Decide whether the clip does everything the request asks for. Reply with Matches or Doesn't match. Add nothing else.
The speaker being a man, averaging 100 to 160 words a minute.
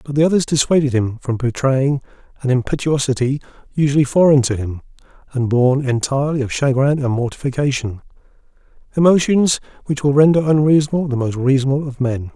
Matches